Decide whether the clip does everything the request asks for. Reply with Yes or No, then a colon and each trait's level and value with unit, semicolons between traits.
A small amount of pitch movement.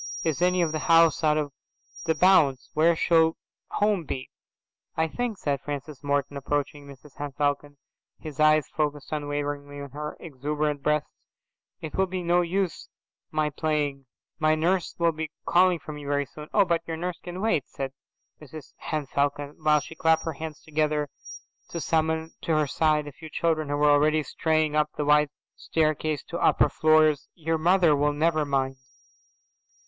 Yes: narrow, 1.9 semitones